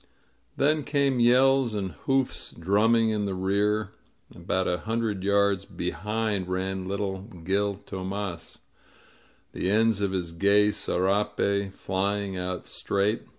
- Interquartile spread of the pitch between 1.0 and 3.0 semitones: Yes, narrow, 2.4 semitones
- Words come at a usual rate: No, slow, 120 wpm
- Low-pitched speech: Yes, low, 100 Hz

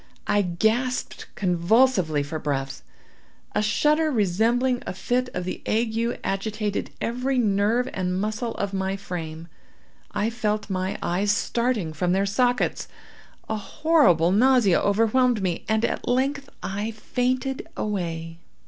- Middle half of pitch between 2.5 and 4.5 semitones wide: No, average, 5.1 semitones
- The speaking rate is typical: No, slow, 115 wpm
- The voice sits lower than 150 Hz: No, high, 210 Hz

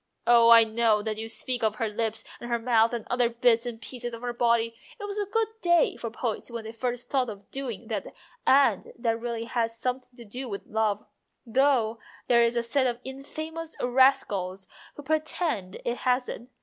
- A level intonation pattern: Yes, narrow, 2.3 semitones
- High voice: Yes, high, 235 Hz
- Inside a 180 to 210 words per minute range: Yes, average, 200 wpm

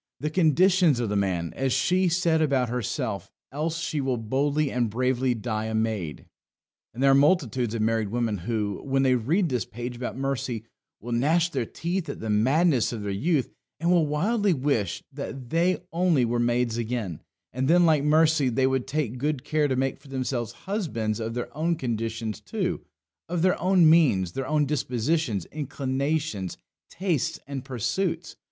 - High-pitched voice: No, low, 135 Hz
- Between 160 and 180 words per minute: Yes, average, 175 wpm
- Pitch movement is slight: No, average, 5.3 semitones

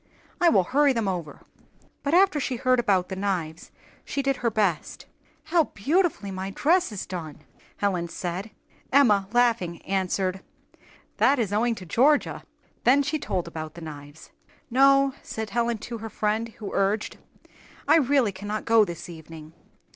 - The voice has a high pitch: Yes, high, 210 Hz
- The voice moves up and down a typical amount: No, wide, 6.0 semitones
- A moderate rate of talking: Yes, average, 155 wpm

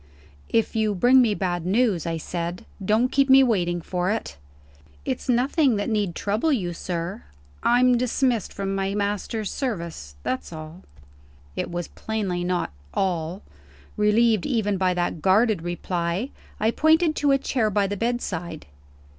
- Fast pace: No, average, 150 wpm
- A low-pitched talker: No, high, 205 Hz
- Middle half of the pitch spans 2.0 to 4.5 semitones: No, average, 5.2 semitones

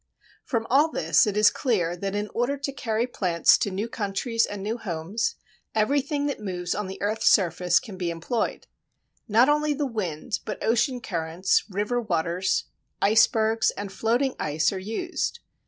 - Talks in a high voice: Yes, high, 215 Hz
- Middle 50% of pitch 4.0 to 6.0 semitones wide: Yes, average, 4.5 semitones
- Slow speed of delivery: No, average, 165 wpm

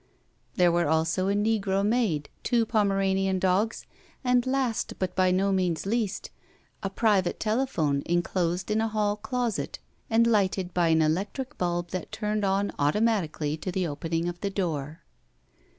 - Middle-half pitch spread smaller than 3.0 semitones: No, average, 3.6 semitones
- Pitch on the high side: Yes, high, 195 Hz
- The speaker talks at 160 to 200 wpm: No, average, 150 wpm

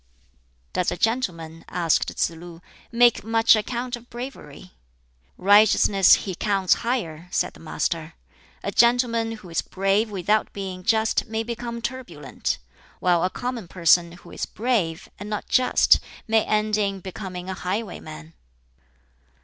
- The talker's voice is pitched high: Yes, high, 200 Hz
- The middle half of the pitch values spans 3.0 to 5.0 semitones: Yes, average, 4.6 semitones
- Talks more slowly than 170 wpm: Yes, average, 140 wpm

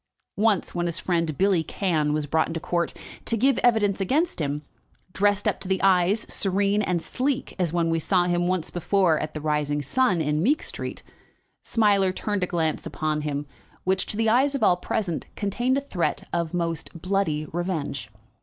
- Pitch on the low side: No, medium, 180 Hz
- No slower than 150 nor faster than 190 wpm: Yes, average, 185 wpm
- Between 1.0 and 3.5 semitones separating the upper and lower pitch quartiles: No, average, 4.2 semitones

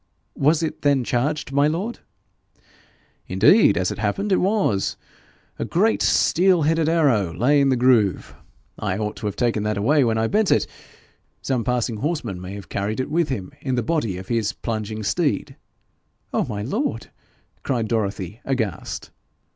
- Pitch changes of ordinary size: No, wide, 6.4 semitones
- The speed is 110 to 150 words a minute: No, average, 165 wpm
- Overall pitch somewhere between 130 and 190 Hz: No, low, 120 Hz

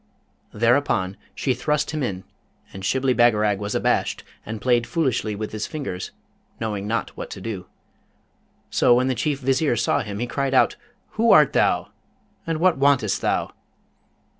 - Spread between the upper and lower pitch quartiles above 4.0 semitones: Yes, average, 4.6 semitones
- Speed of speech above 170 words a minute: No, average, 160 wpm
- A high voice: No, low, 120 Hz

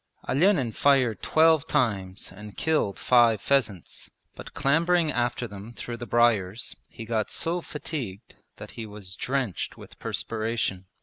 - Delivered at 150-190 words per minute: No, slow, 135 wpm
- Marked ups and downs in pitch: No, average, 5.0 semitones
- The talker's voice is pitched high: No, low, 120 Hz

